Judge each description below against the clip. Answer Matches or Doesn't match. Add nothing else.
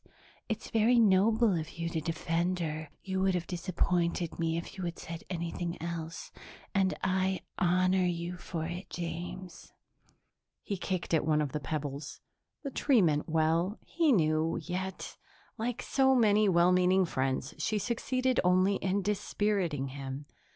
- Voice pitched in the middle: Matches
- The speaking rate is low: Doesn't match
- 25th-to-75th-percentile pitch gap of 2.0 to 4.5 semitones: Matches